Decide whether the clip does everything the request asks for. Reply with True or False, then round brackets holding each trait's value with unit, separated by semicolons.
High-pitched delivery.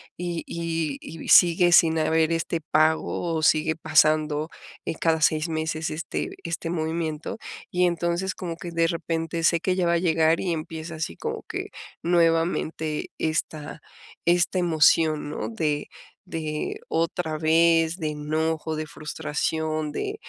False (160 Hz)